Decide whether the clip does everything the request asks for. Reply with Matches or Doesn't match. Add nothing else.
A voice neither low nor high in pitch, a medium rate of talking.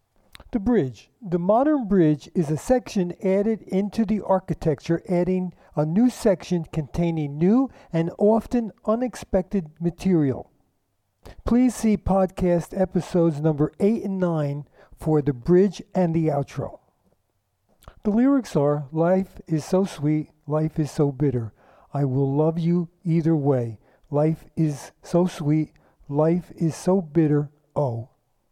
Doesn't match